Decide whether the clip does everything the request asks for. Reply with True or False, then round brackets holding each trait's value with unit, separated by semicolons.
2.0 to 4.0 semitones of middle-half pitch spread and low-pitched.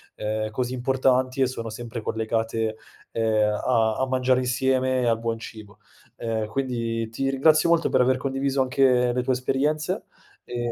True (2.6 semitones; 125 Hz)